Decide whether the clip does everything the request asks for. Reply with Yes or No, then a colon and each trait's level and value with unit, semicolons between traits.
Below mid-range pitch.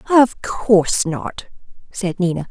No: high, 195 Hz